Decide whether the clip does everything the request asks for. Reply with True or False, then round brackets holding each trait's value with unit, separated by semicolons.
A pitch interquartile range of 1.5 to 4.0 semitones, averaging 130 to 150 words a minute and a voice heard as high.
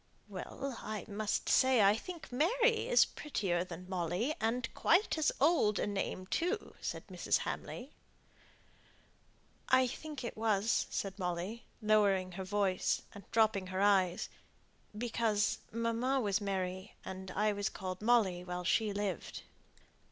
False (4.4 semitones; 135 wpm; 210 Hz)